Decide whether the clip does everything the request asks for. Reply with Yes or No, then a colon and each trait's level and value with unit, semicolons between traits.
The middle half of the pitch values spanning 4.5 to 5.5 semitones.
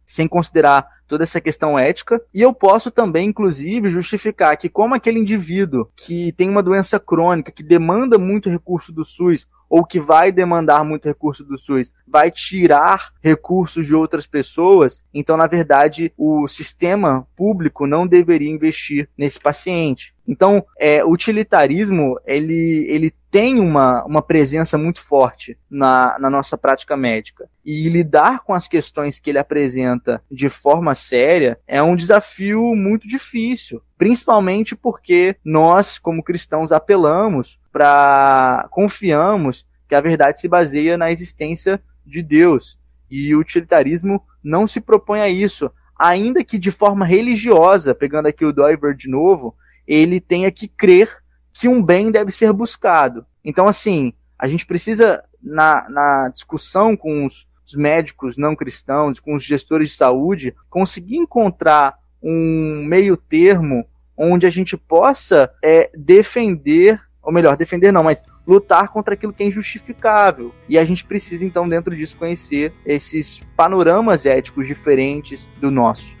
Yes: average, 5.2 semitones